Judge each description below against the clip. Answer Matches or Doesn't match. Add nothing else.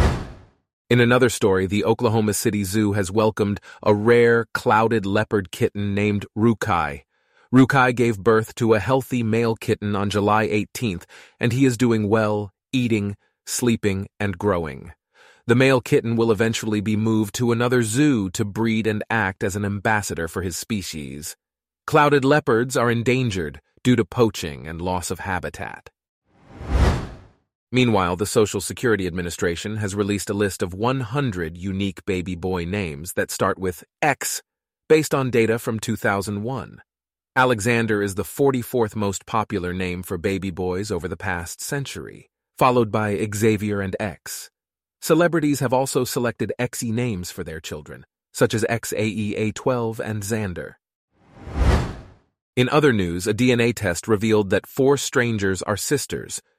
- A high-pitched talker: Doesn't match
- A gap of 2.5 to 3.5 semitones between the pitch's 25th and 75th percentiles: Matches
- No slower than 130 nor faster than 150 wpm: Matches